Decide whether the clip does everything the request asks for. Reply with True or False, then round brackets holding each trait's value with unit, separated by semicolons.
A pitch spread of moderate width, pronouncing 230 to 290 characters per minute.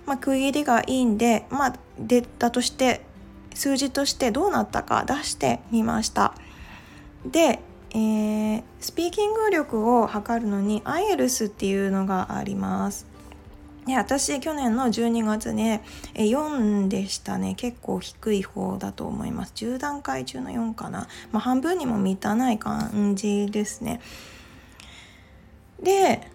True (4.4 semitones; 250 characters per minute)